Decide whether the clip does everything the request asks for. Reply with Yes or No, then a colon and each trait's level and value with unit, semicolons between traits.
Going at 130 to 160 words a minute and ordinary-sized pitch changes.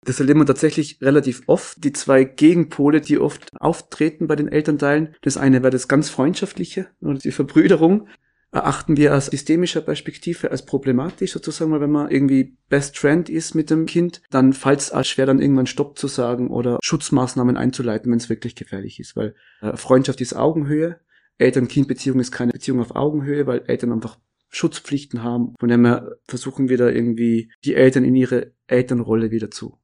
No: average, 175 wpm; average, 3.4 semitones